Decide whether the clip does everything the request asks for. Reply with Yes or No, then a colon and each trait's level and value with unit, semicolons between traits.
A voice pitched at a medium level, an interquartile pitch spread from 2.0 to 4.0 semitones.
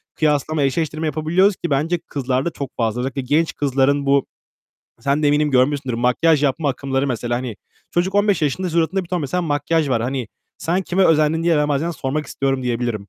Yes: medium, 145 Hz; average, 3.6 semitones